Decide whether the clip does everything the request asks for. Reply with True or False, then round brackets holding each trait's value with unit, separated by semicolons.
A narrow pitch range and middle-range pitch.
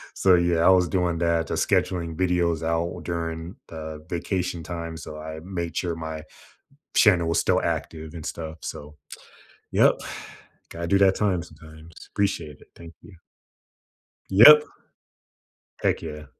False (1.9 semitones; 85 Hz)